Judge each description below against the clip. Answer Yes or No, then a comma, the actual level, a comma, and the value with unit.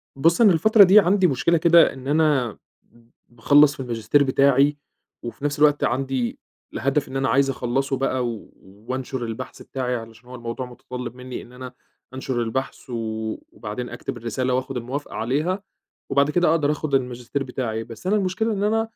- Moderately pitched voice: No, low, 130 Hz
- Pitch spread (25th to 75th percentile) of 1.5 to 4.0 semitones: Yes, average, 3.5 semitones